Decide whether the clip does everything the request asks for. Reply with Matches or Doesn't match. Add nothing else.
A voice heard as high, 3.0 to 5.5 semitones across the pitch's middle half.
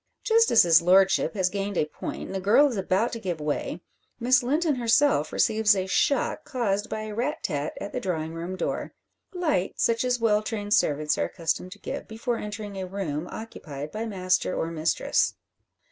Matches